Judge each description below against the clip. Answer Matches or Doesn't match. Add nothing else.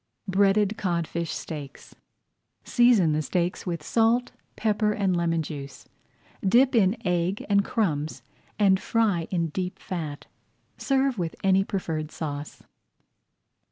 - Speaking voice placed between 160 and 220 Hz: Matches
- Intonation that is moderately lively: Matches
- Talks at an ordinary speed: Doesn't match